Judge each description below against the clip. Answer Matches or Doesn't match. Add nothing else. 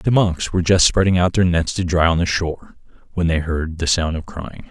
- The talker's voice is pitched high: Doesn't match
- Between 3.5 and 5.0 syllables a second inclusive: Doesn't match